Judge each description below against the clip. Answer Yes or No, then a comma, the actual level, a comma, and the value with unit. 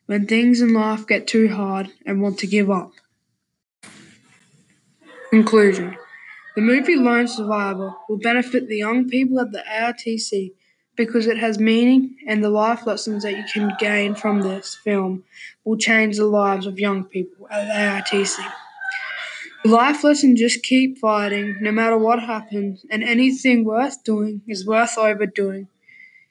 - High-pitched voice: Yes, high, 220 Hz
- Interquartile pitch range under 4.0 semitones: Yes, average, 2.7 semitones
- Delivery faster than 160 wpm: No, average, 155 wpm